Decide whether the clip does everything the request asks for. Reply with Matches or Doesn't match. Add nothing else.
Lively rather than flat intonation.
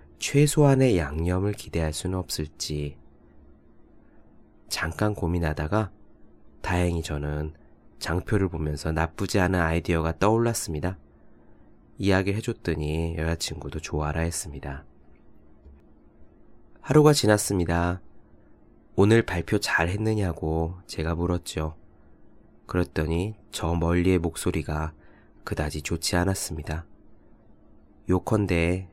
Doesn't match